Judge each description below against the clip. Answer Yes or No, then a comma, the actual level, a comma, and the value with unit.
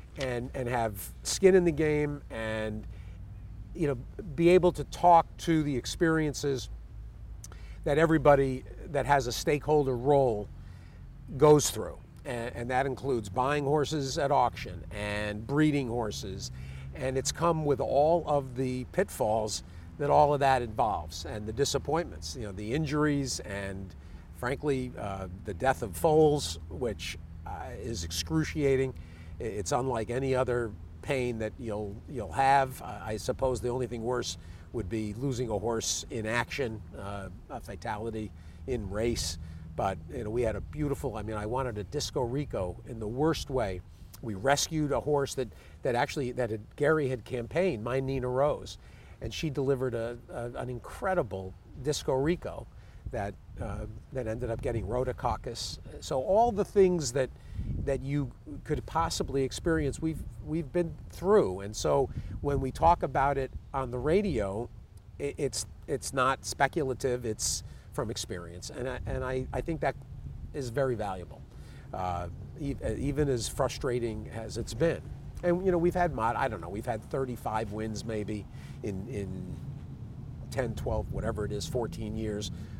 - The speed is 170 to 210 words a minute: No, average, 155 wpm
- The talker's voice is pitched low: Yes, low, 120 Hz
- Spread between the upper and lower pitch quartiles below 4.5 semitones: No, average, 5.2 semitones